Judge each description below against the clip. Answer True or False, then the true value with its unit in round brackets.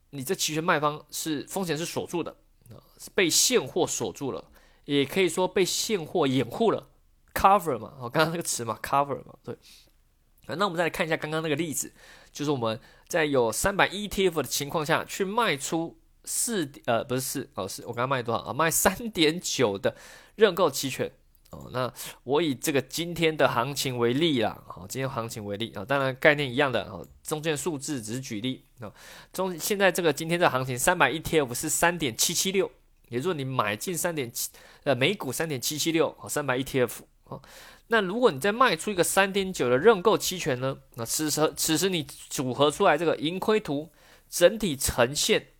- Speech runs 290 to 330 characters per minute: True (305 characters per minute)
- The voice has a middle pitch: True (150 Hz)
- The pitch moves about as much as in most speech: True (5.0 semitones)